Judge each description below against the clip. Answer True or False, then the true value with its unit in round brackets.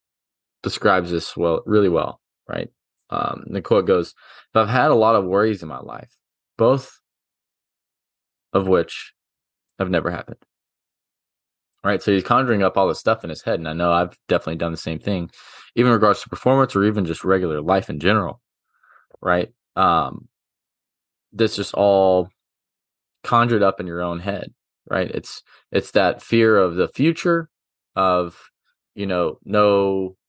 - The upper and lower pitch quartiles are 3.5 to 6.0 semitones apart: True (4.0 semitones)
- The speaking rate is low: False (160 wpm)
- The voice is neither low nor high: False (100 Hz)